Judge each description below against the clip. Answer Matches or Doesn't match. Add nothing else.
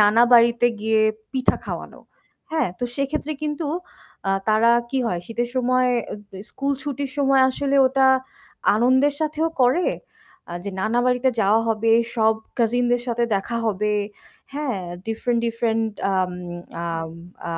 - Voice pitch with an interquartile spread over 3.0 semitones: Matches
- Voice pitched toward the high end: Matches